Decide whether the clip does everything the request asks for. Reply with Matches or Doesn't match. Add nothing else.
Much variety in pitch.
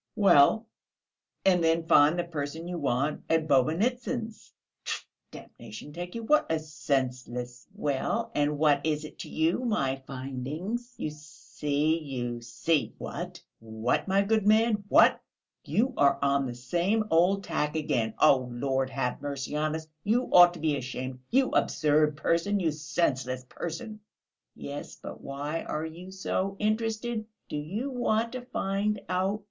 Matches